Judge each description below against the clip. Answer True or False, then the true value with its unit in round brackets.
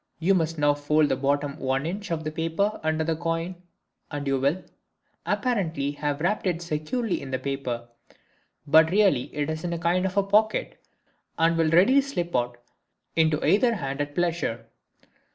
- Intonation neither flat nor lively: True (3.6 semitones)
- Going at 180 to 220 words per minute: False (170 wpm)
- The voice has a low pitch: False (160 Hz)